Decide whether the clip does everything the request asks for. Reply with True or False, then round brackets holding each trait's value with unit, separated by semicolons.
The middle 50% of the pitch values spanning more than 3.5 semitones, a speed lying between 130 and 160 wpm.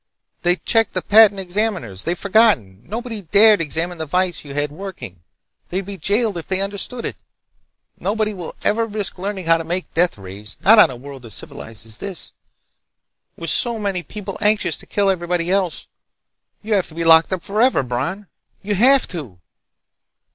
False (4.4 semitones; 170 wpm)